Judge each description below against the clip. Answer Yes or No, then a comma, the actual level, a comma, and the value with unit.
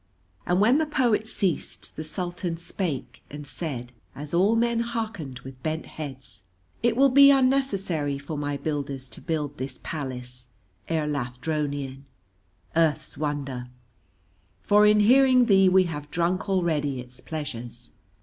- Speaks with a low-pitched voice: No, medium, 155 Hz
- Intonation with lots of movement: Yes, wide, 6.6 semitones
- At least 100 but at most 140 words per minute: Yes, slow, 135 wpm